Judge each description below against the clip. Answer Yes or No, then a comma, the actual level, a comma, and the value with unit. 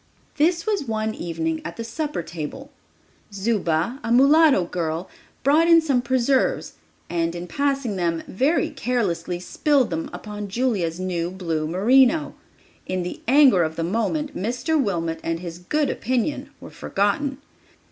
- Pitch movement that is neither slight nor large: No, wide, 8.0 semitones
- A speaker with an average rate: Yes, average, 145 wpm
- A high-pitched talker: Yes, high, 215 Hz